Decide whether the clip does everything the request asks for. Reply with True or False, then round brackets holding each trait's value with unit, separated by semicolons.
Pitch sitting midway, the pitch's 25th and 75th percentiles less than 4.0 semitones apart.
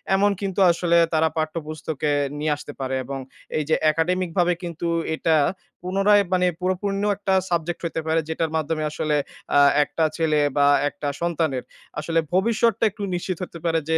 True (165 Hz; 2.8 semitones)